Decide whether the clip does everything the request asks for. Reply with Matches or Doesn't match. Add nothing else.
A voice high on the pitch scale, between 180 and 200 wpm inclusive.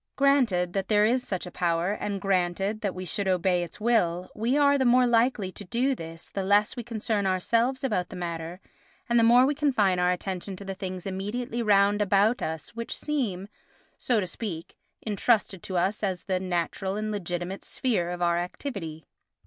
Matches